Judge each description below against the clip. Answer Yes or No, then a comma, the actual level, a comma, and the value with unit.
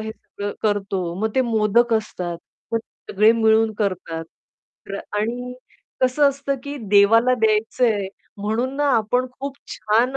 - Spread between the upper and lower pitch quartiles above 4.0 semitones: No, average, 3.3 semitones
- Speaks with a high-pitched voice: Yes, high, 220 Hz